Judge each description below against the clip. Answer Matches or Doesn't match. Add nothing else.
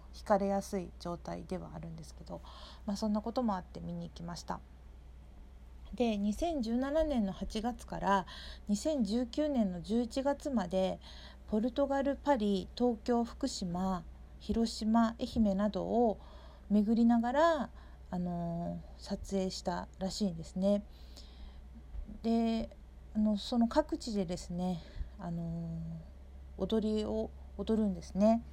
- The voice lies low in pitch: Doesn't match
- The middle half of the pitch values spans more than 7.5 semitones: Doesn't match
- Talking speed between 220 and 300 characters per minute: Matches